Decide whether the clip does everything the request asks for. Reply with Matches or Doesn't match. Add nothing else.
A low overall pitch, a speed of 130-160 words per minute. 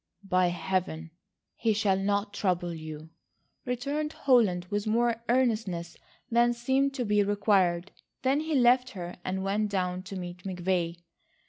Doesn't match